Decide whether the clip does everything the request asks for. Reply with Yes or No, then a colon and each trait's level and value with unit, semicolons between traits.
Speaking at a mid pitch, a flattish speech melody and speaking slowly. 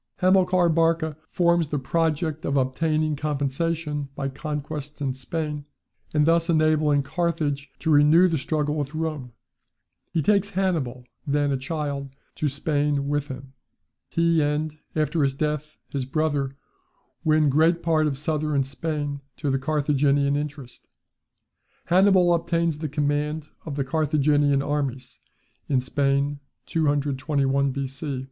Yes: medium, 150 Hz; narrow, 2.3 semitones; slow, 130 wpm